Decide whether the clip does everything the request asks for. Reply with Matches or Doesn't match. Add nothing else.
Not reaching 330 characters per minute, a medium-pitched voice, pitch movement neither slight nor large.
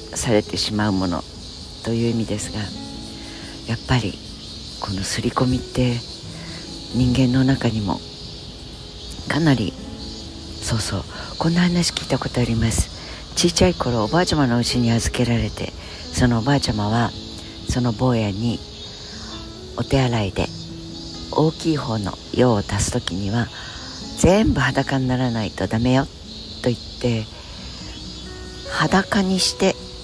Doesn't match